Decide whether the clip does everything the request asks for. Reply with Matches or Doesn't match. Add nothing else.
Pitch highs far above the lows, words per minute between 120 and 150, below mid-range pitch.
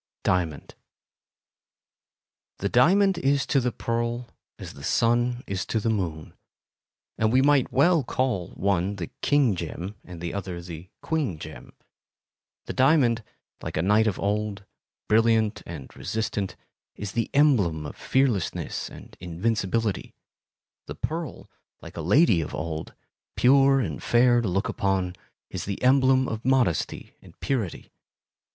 Matches